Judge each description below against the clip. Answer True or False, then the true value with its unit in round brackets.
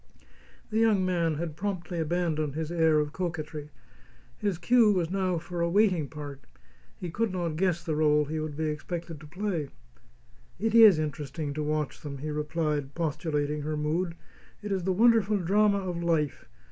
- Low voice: False (165 Hz)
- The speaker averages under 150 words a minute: False (170 wpm)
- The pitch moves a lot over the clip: False (3.5 semitones)